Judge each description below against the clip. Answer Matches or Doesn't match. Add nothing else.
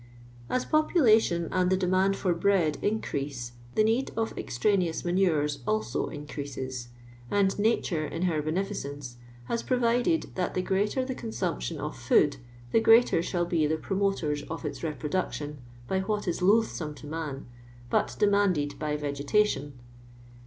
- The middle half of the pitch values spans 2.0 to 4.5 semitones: Doesn't match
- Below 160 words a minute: Matches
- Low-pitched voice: Doesn't match